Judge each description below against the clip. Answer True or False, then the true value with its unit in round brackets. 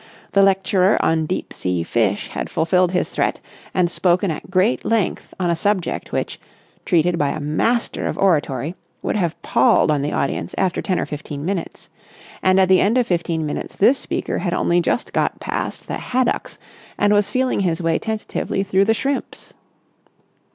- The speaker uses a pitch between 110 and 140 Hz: False (185 Hz)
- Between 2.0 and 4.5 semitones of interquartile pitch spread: True (3.7 semitones)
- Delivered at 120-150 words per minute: False (180 wpm)